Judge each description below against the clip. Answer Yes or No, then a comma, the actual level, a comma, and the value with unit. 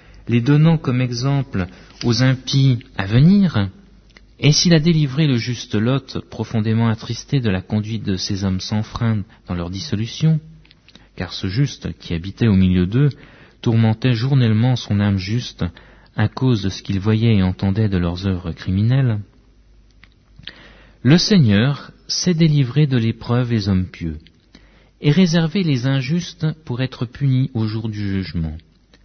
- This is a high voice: No, low, 115 Hz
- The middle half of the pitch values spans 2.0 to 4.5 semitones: No, wide, 5.6 semitones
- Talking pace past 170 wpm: No, average, 150 wpm